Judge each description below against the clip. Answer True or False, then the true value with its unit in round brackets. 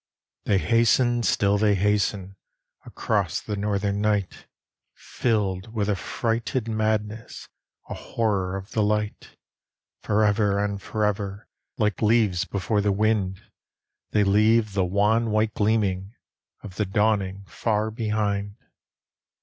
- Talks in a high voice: False (105 Hz)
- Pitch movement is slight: True (1.7 semitones)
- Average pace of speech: False (115 wpm)